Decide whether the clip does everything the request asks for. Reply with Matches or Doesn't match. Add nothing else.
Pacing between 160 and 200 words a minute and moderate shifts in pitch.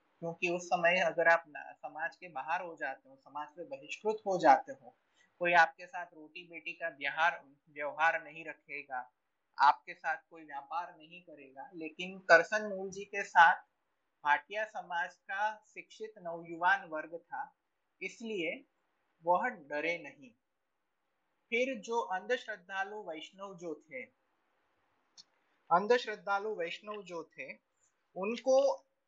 Doesn't match